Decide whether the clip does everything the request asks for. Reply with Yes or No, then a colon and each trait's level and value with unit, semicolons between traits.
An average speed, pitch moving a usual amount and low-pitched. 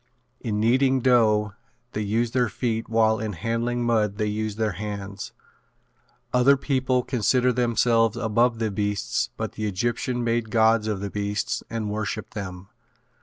No: average, 150 wpm; narrow, 2.3 semitones; low, 110 Hz